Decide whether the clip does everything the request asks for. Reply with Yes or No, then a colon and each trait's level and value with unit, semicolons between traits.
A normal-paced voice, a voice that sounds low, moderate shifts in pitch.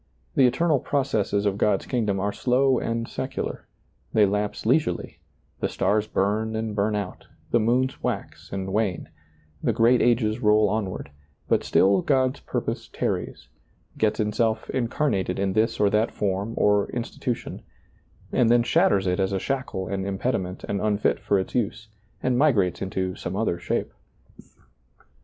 Yes: average, 160 wpm; low, 105 Hz; average, 3.4 semitones